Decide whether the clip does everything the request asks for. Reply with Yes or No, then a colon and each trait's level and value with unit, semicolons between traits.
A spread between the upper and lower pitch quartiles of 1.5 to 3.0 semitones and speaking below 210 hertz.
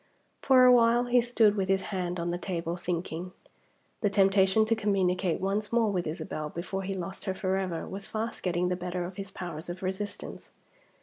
Yes: average, 2.7 semitones; high, 190 Hz